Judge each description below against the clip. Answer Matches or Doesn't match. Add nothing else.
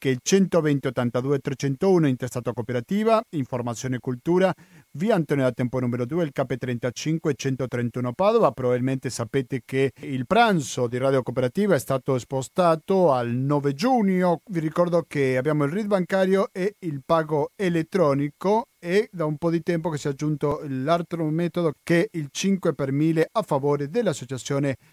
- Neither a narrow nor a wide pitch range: Matches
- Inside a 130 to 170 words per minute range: Matches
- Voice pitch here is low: Doesn't match